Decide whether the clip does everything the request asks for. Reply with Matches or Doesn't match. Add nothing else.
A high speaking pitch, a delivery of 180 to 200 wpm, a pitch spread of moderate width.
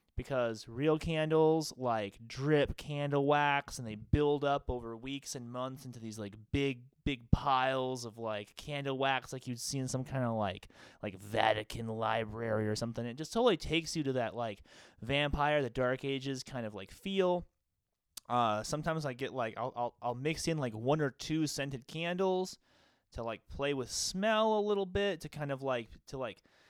Doesn't match